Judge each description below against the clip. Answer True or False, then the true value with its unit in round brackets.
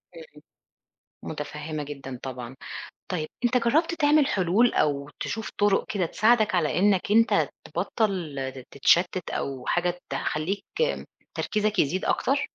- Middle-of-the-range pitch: True (180 Hz)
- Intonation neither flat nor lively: False (7.0 semitones)